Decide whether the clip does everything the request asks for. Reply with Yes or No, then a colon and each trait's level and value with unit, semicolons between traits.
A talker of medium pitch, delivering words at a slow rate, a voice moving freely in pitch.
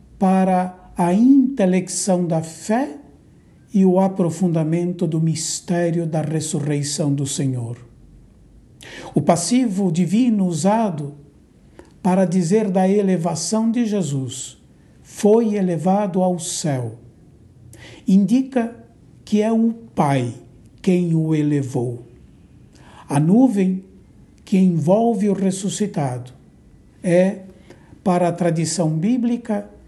No: medium, 180 Hz; slow, 95 wpm; average, 4.5 semitones